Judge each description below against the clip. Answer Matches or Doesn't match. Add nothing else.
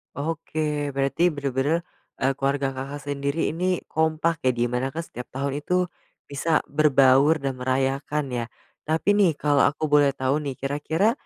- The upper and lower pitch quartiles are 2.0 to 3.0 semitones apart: Matches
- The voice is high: Doesn't match